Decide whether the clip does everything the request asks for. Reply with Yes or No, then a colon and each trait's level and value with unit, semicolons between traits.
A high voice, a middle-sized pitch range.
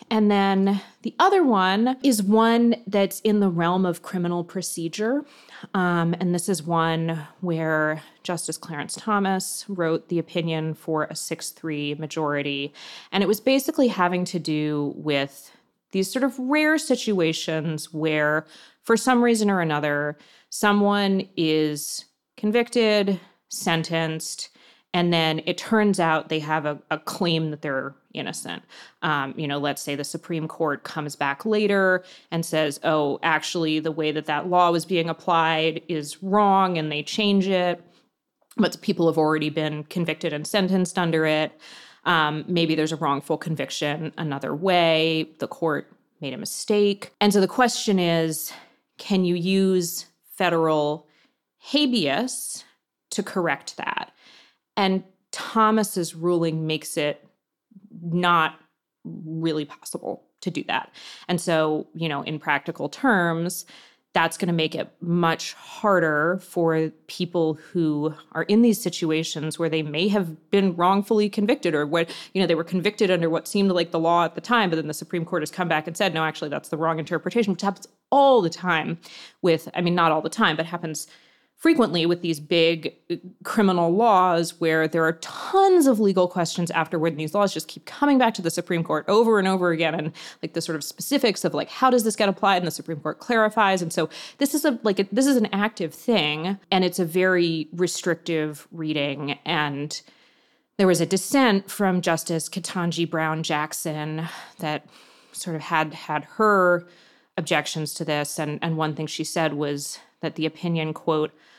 No: medium, 170 Hz; average, 3.8 semitones